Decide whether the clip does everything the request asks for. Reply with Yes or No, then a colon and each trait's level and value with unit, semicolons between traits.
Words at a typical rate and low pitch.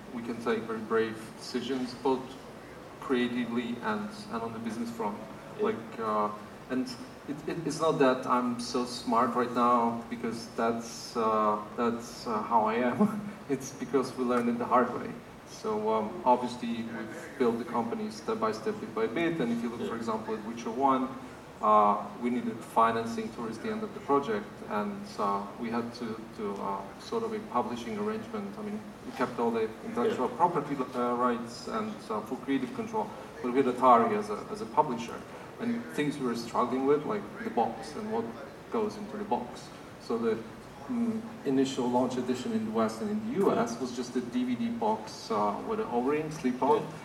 Yes: average, 190 wpm; low, 125 Hz